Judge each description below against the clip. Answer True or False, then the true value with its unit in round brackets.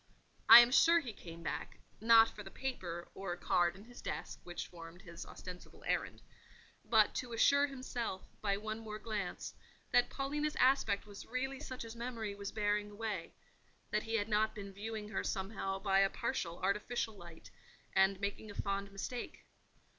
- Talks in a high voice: True (210 Hz)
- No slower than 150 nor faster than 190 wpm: True (165 wpm)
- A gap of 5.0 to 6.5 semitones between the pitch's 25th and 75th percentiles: False (3.2 semitones)